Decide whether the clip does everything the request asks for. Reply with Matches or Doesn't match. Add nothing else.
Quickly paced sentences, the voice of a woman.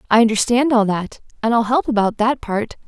Matches